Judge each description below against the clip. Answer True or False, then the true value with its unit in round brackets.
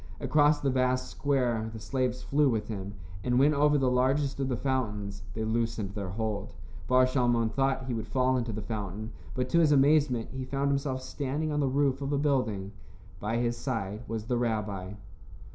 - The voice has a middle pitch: False (125 Hz)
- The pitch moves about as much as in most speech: True (3.7 semitones)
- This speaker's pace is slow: False (195 wpm)